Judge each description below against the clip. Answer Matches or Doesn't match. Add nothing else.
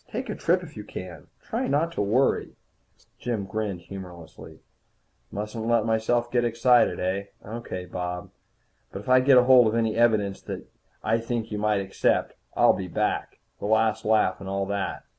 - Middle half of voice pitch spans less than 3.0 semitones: Doesn't match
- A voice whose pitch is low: Matches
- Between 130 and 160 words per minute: Doesn't match